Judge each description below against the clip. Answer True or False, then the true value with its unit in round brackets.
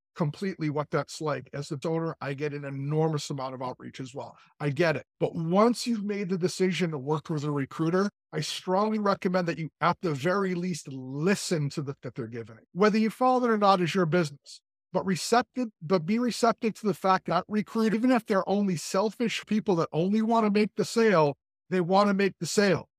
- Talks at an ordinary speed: False (220 wpm)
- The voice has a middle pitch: True (180 Hz)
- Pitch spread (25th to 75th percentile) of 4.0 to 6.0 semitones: True (5.2 semitones)